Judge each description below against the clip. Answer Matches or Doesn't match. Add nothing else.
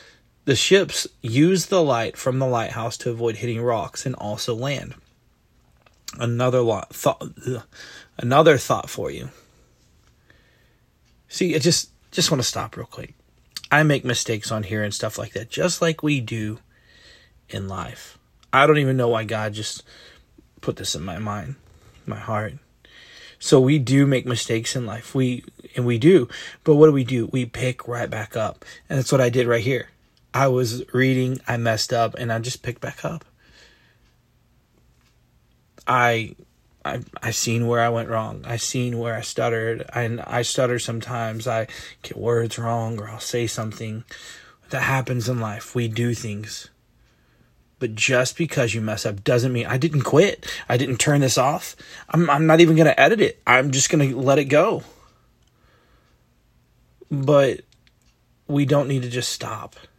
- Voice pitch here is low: Matches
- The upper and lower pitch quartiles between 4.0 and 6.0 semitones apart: Doesn't match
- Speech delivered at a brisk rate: Doesn't match